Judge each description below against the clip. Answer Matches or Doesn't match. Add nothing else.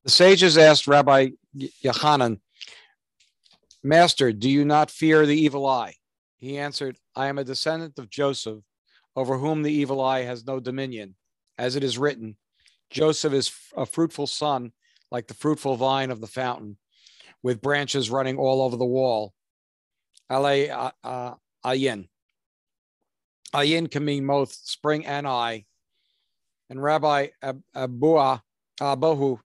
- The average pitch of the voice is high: Doesn't match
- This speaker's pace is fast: Doesn't match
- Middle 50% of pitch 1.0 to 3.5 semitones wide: Matches